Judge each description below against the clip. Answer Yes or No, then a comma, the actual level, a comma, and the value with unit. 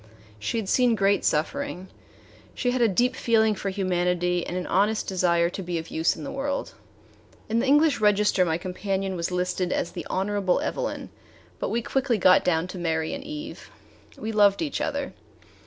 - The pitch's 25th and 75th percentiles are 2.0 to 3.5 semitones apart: No, average, 4.8 semitones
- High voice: Yes, high, 195 Hz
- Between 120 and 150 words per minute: No, average, 185 wpm